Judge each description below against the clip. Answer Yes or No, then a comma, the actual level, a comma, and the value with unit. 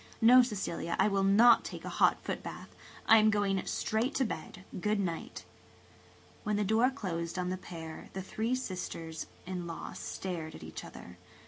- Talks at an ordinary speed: Yes, average, 175 wpm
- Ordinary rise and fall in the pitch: Yes, average, 4.2 semitones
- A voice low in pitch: No, high, 195 Hz